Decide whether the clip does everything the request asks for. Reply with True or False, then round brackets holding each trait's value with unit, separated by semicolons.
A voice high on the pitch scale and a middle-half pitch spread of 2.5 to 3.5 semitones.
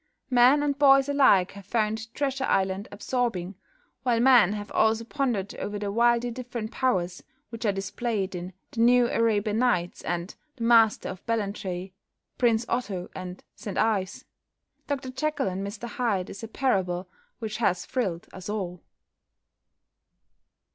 False (220 Hz; 4.2 semitones)